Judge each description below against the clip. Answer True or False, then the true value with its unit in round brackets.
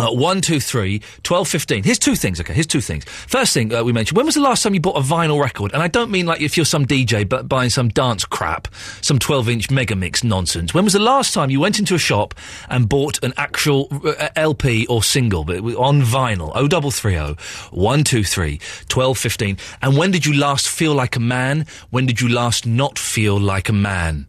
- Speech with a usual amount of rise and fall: False (6.3 semitones)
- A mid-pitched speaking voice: False (130 Hz)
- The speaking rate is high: True (230 wpm)